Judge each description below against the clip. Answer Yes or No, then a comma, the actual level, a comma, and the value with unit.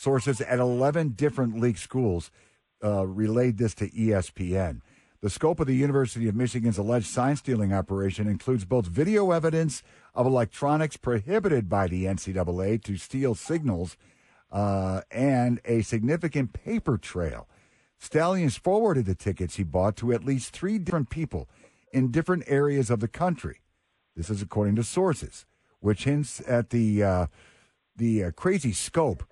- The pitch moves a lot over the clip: Yes, wide, 5.7 semitones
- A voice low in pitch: Yes, low, 120 Hz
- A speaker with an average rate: Yes, average, 150 wpm